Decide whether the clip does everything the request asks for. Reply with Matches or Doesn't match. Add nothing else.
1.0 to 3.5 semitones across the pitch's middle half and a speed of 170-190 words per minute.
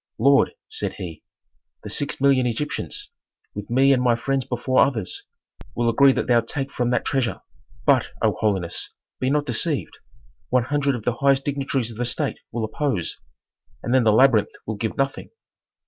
Matches